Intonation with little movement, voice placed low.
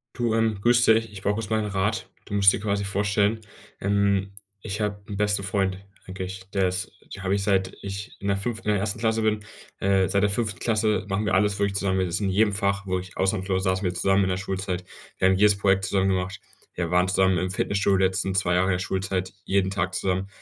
Yes: narrow, 1.6 semitones; low, 100 Hz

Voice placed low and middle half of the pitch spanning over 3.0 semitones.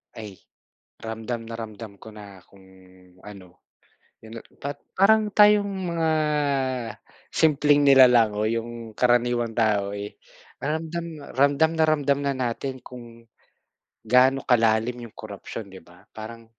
Yes: low, 120 Hz; average, 4.2 semitones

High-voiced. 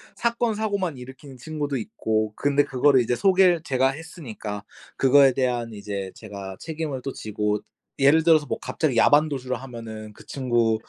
No: low, 130 Hz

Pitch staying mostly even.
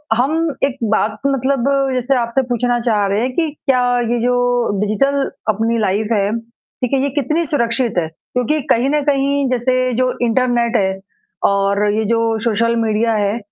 No: average, 3.3 semitones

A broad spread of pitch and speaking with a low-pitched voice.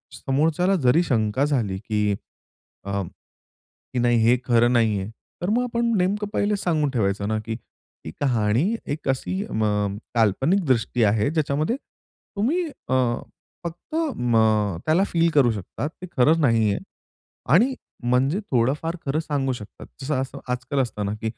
Yes: wide, 6.9 semitones; low, 130 Hz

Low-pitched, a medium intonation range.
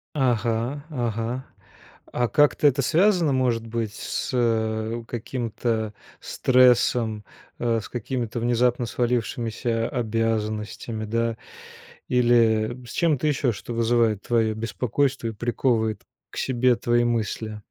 No: low, 120 Hz; narrow, 1.8 semitones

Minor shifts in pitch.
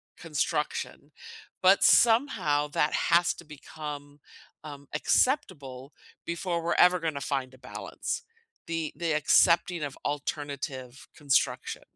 No: average, 3.3 semitones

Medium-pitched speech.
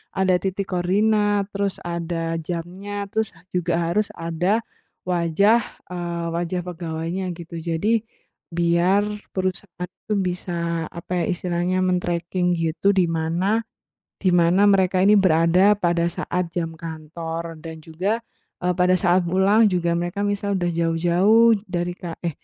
Yes: medium, 180 Hz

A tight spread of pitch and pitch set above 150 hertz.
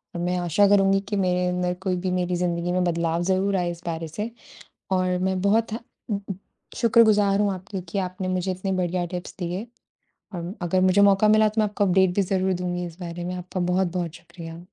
Yes: narrow, 1.8 semitones; medium, 185 Hz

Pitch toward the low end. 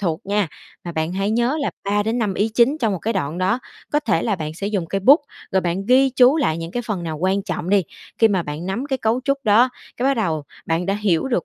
No: high, 200 Hz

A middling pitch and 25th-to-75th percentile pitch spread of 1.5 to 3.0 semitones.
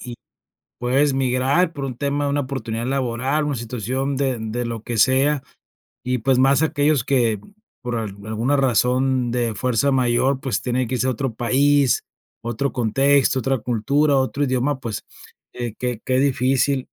No: low, 130 Hz; narrow, 2.5 semitones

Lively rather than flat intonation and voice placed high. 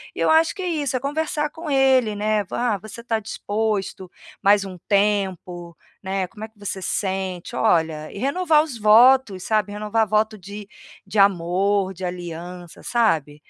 No: average, 4.0 semitones; high, 205 Hz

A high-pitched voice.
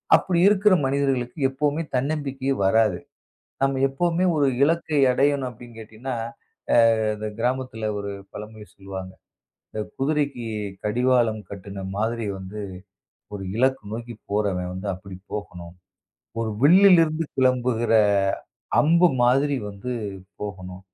No: low, 120 Hz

